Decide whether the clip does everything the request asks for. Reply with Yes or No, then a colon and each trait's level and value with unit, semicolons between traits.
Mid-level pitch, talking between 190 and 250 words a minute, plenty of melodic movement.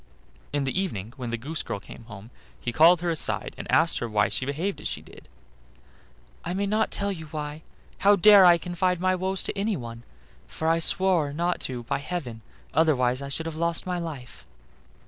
Yes: medium, 160 Hz; average, 200 wpm; wide, 6.0 semitones